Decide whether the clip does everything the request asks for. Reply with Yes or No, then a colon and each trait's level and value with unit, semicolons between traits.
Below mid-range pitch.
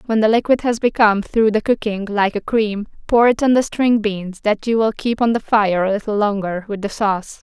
No: high, 215 Hz